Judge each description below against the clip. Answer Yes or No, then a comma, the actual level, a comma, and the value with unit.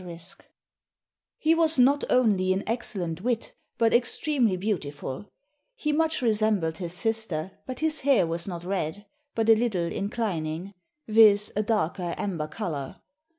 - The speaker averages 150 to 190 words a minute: No, average, 140 wpm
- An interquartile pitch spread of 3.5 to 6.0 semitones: Yes, wide, 5.5 semitones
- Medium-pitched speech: No, high, 205 Hz